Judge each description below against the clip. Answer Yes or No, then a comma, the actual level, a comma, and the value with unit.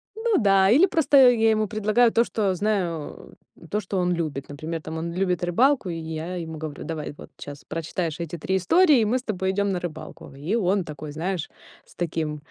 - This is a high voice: No, medium, 180 Hz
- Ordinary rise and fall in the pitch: Yes, average, 5.0 semitones